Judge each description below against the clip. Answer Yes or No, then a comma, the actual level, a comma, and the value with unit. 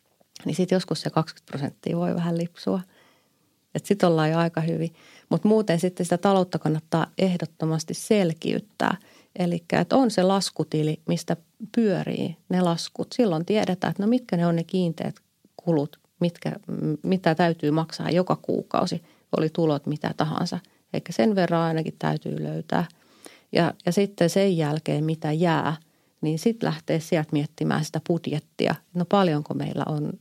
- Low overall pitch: No, medium, 170 Hz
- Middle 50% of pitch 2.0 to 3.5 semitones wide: Yes, average, 2.8 semitones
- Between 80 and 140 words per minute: No, fast, 155 wpm